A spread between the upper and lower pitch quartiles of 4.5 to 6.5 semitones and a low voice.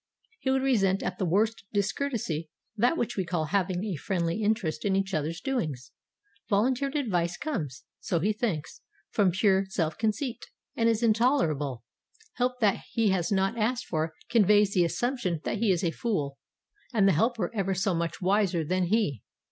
No: average, 5.0 semitones; high, 195 Hz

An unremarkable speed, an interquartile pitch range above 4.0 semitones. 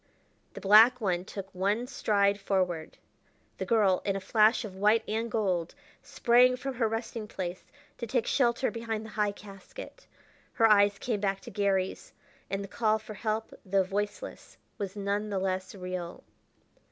No: average, 165 wpm; narrow, 2.6 semitones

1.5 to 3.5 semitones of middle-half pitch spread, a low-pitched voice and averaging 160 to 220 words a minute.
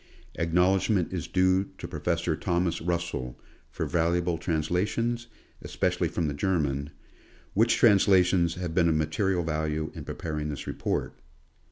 No: average, 2.9 semitones; very low, 85 Hz; average, 140 wpm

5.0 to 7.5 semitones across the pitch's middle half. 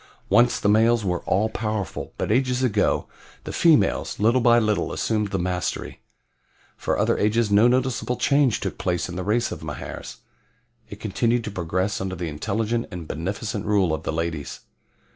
No: average, 4.2 semitones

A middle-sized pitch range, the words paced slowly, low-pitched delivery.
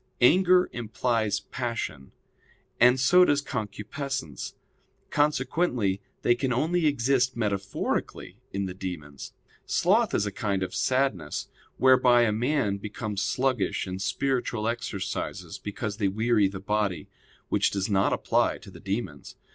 Yes: average, 4.8 semitones; slow, 130 wpm; low, 110 Hz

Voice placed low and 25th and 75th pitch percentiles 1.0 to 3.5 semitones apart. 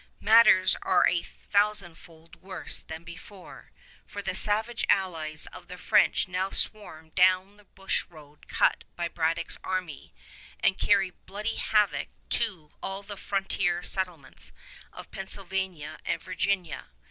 No: medium, 185 Hz; average, 2.9 semitones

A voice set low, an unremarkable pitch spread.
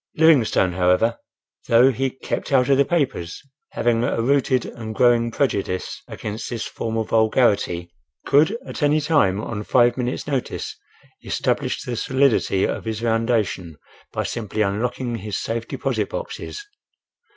Yes: low, 115 Hz; average, 3.6 semitones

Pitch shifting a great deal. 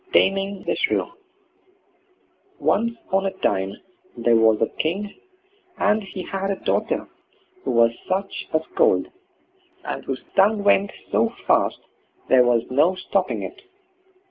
Yes: wide, 8.4 semitones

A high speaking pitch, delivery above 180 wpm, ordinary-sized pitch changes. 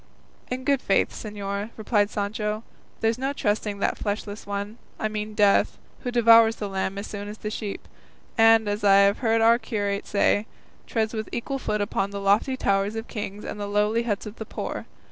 No: high, 210 Hz; average, 195 wpm; narrow, 1.8 semitones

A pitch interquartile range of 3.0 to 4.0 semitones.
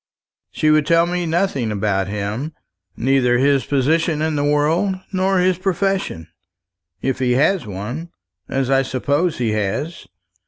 No: wide, 5.5 semitones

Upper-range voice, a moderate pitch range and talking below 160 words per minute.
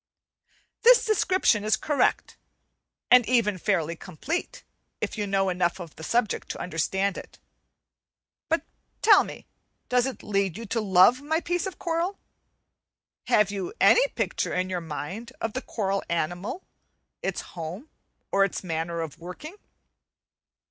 No: high, 205 Hz; wide, 7.7 semitones; average, 140 wpm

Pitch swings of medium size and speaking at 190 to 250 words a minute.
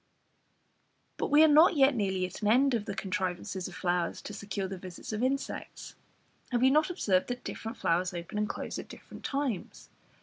No: wide, 6.3 semitones; average, 195 wpm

